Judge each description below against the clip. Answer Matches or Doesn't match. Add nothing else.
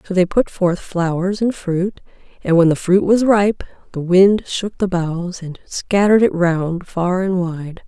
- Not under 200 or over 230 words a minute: Doesn't match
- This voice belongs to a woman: Matches